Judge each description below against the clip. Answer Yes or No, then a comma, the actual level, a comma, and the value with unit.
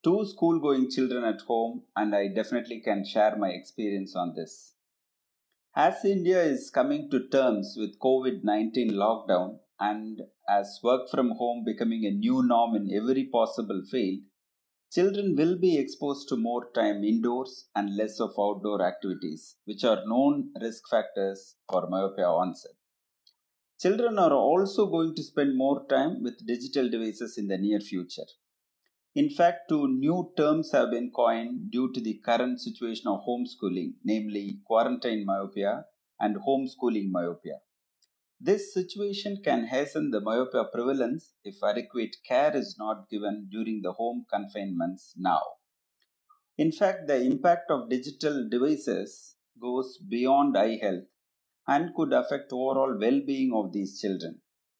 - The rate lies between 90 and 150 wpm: Yes, average, 140 wpm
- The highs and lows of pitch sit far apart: Yes, wide, 7.8 semitones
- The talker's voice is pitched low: Yes, low, 125 Hz